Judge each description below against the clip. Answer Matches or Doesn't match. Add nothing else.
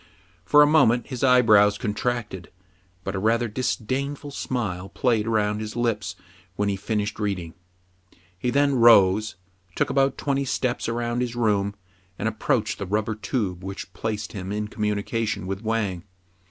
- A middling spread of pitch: Matches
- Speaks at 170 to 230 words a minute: Doesn't match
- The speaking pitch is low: Matches